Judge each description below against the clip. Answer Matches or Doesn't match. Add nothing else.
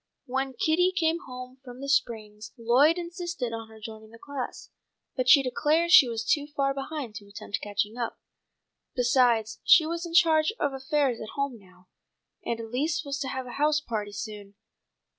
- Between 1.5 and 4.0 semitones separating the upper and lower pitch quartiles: Doesn't match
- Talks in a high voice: Matches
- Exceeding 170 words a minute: Matches